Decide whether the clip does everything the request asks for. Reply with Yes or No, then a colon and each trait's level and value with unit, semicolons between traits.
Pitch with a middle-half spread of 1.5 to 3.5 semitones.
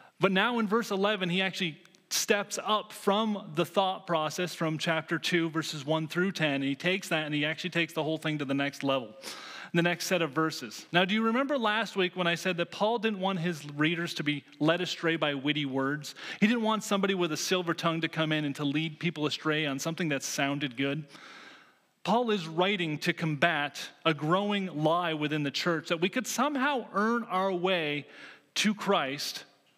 No: average, 4.2 semitones